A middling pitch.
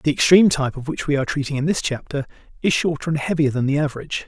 Yes: medium, 145 Hz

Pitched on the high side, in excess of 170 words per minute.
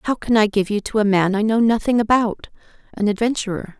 Yes: high, 215 Hz; fast, 205 wpm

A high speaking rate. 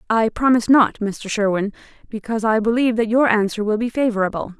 No: average, 170 wpm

